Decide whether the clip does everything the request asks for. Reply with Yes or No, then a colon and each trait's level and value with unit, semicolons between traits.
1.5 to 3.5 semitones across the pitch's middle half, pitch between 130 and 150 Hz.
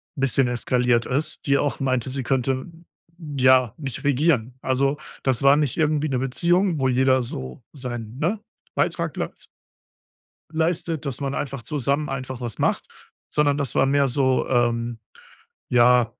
Yes: narrow, 2.5 semitones; low, 135 Hz